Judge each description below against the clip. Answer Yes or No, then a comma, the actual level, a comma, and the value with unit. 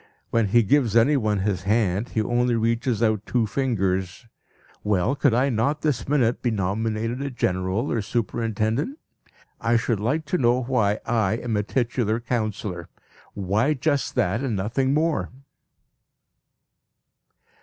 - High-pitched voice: No, low, 115 Hz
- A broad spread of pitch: No, average, 3.4 semitones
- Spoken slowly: No, average, 145 wpm